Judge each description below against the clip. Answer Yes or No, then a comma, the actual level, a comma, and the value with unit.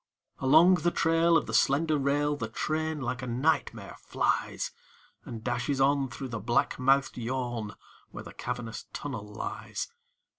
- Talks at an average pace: Yes, average, 150 wpm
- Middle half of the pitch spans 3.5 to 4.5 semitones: Yes, average, 4.1 semitones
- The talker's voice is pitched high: No, low, 135 Hz